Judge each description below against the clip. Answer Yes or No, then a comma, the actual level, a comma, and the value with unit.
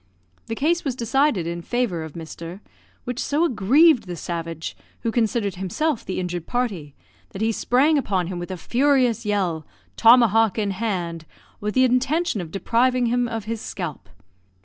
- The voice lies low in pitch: No, high, 220 Hz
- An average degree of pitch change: No, wide, 5.9 semitones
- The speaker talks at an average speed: Yes, average, 165 wpm